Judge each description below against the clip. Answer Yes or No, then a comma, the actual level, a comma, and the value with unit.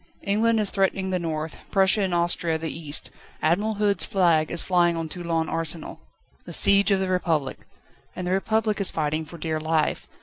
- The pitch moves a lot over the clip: No, average, 3.4 semitones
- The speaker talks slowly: No, average, 180 wpm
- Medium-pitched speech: Yes, medium, 175 Hz